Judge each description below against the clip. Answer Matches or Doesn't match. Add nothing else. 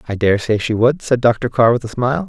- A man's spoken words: Matches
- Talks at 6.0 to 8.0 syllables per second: Doesn't match